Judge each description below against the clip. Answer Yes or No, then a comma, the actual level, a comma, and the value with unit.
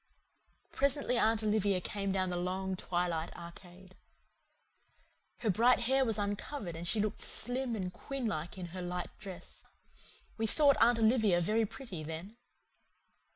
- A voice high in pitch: Yes, high, 200 Hz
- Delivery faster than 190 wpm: No, average, 145 wpm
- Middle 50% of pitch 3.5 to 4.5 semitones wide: Yes, average, 4.2 semitones